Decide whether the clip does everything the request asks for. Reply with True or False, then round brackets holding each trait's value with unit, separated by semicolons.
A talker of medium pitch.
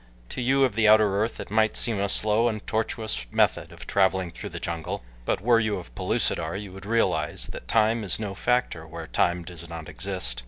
False (100 Hz)